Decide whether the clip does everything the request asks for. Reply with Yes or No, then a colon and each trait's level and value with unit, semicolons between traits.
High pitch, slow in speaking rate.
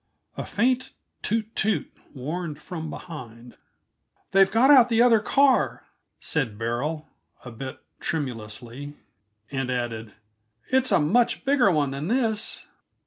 No: medium, 160 Hz; slow, 125 wpm